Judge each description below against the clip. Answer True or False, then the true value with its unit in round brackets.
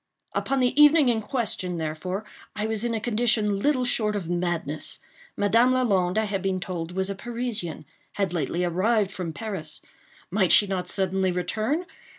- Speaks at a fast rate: False (160 wpm)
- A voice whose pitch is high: True (200 Hz)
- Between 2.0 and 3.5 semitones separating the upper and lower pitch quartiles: False (4.3 semitones)